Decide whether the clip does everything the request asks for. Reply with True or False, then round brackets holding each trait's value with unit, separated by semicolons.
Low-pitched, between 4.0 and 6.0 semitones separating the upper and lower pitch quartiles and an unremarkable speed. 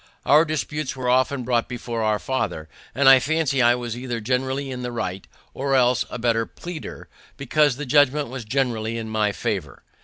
False (125 Hz; 2.9 semitones; 185 wpm)